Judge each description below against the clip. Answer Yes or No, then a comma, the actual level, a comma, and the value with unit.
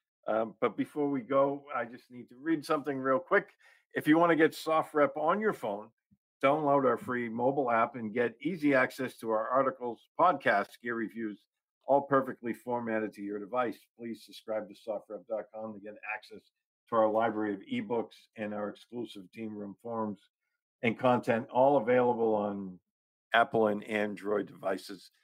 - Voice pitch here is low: Yes, low, 120 Hz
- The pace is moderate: Yes, average, 165 wpm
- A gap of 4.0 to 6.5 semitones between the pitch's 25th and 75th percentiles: Yes, average, 4.5 semitones